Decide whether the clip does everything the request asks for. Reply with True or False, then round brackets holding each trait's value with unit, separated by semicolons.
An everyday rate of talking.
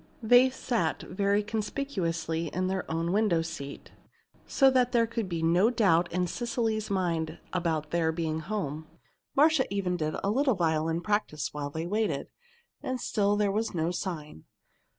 True (160 wpm)